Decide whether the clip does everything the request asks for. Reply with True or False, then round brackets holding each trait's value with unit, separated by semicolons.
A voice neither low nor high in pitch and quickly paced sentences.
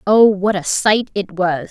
False (195 Hz; 210 wpm)